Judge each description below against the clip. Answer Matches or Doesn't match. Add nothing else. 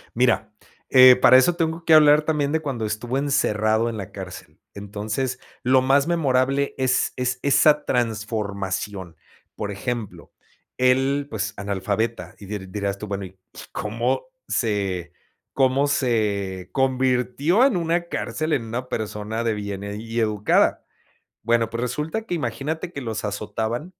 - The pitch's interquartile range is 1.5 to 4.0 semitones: Doesn't match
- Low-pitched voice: Matches